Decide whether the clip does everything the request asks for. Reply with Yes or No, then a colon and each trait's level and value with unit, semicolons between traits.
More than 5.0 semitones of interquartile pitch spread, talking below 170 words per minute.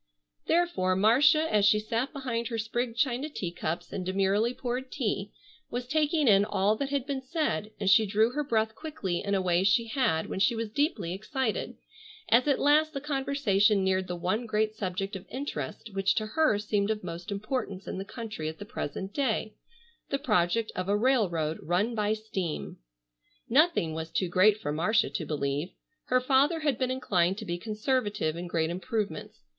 No: wide, 5.5 semitones; average, 185 wpm